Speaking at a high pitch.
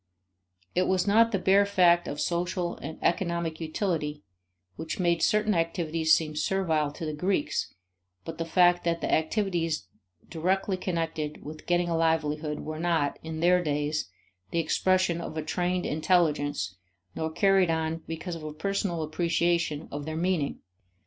No: medium, 165 Hz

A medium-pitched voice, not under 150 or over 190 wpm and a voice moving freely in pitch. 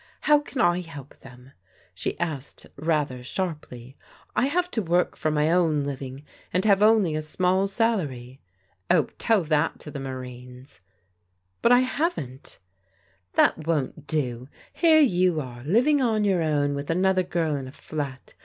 Yes: medium, 155 Hz; average, 170 wpm; wide, 6.4 semitones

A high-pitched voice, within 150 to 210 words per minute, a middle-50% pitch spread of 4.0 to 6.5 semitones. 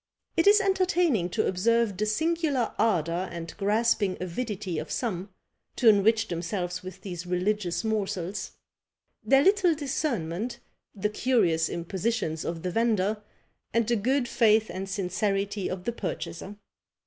No: high, 210 Hz; slow, 135 wpm; average, 4.5 semitones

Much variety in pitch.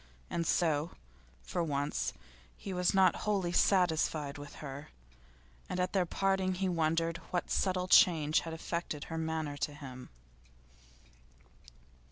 No: average, 3.3 semitones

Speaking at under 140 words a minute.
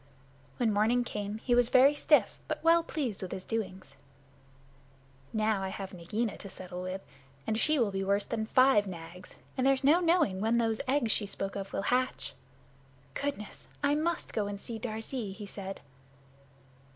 No: average, 175 wpm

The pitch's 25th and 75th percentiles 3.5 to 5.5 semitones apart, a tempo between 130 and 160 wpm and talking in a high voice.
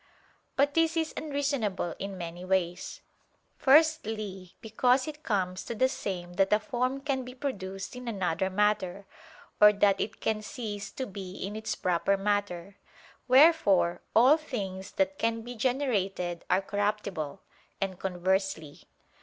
Yes: average, 4.9 semitones; average, 140 wpm; high, 205 Hz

